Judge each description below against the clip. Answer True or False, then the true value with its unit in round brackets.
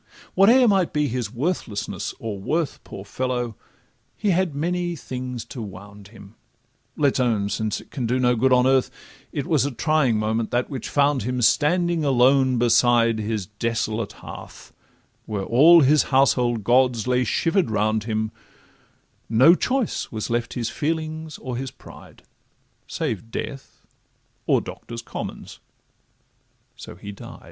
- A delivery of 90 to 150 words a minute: True (135 wpm)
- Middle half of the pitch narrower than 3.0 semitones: False (4.9 semitones)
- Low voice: True (125 Hz)